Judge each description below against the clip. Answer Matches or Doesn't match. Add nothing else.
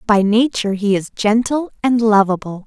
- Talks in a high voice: Matches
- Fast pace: Doesn't match